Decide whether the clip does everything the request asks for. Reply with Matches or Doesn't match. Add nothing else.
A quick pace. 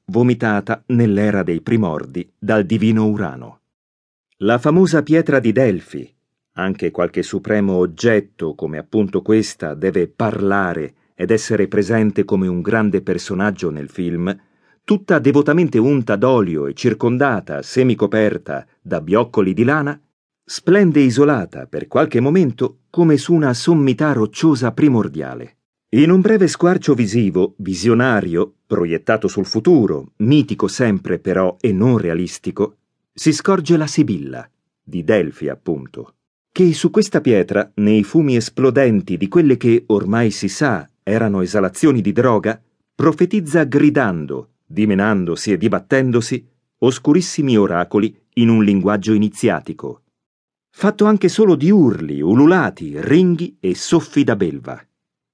Doesn't match